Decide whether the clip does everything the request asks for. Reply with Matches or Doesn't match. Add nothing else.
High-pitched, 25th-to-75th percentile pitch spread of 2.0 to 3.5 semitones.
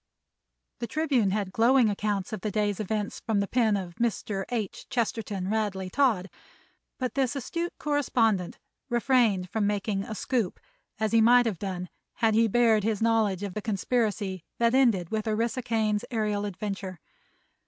Matches